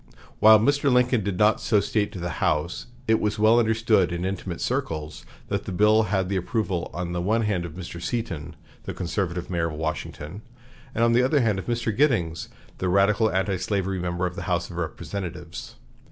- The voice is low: Yes, very low, 95 Hz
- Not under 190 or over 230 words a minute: Yes, average, 195 wpm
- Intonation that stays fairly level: No, average, 4.0 semitones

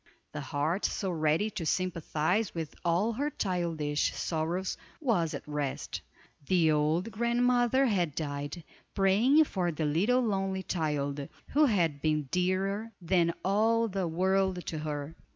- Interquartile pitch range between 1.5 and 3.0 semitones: No, average, 4.9 semitones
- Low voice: No, medium, 180 Hz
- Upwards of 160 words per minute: No, slow, 135 wpm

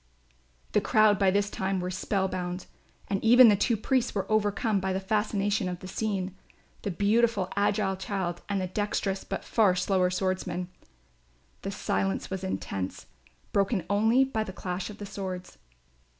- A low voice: No, high, 195 Hz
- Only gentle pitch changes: Yes, narrow, 2.1 semitones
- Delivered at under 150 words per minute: No, average, 165 wpm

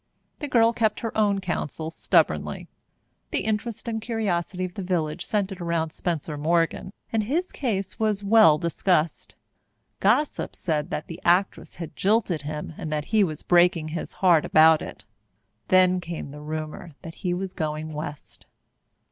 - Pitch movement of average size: Yes, average, 4.6 semitones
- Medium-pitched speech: Yes, medium, 175 Hz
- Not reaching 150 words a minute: No, average, 155 wpm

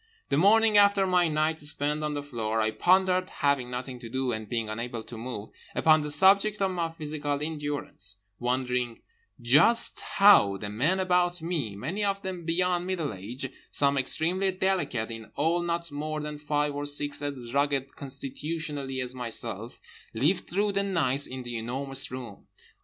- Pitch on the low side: No, medium, 145 Hz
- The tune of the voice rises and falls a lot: Yes, wide, 5.8 semitones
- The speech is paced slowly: No, average, 165 wpm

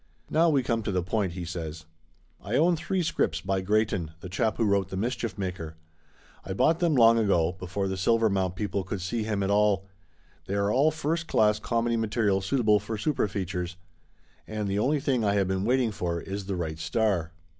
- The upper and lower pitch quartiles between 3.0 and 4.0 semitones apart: Yes, average, 3.7 semitones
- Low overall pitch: Yes, low, 100 Hz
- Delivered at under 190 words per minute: No, fast, 205 wpm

